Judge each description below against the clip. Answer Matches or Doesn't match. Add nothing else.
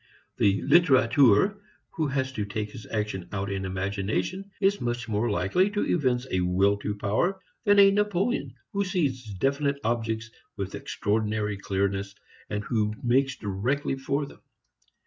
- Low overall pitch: Matches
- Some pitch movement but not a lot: Doesn't match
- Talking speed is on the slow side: Doesn't match